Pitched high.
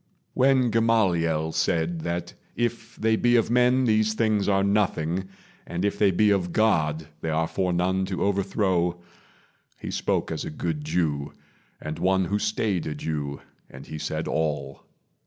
No: very low, 95 Hz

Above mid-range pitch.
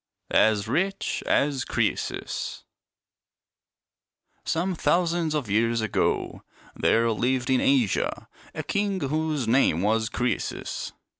No: low, 130 Hz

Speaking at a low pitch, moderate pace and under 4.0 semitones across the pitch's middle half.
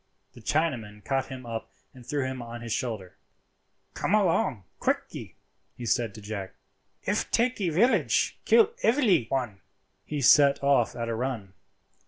No: low, 130 Hz; average, 150 wpm; average, 4.9 semitones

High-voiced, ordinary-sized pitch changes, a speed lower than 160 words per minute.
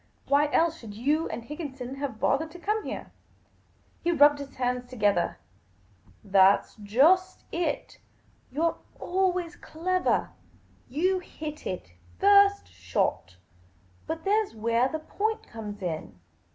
No: very high, 290 Hz; wide, 7.7 semitones; average, 150 wpm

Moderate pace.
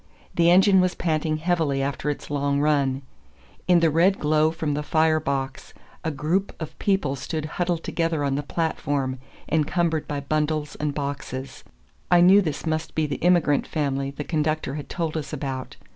Yes: average, 175 wpm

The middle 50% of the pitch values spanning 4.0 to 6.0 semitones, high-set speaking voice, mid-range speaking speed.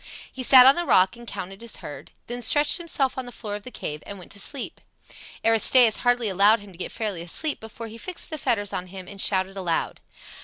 No: average, 4.5 semitones; high, 220 Hz; fast, 230 wpm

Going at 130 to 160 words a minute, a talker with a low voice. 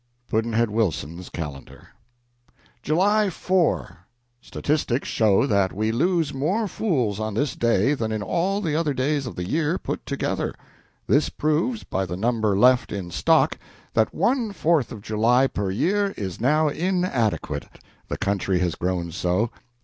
Yes: average, 150 wpm; low, 120 Hz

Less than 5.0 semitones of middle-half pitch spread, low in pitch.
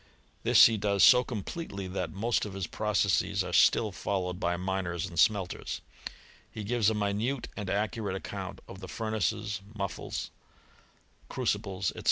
Yes: narrow, 2.5 semitones; low, 100 Hz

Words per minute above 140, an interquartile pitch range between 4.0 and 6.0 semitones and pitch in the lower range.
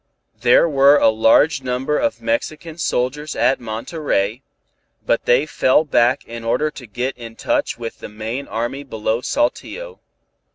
Yes: average, 150 wpm; average, 4.7 semitones; low, 130 Hz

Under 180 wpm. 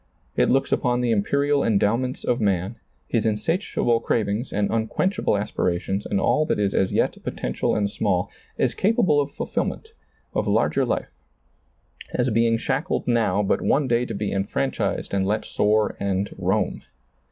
Yes: average, 165 wpm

